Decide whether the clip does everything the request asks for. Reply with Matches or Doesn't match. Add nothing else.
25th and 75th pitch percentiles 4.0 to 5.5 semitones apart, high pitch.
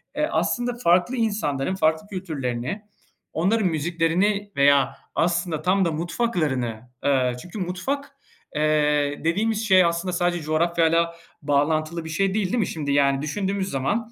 Doesn't match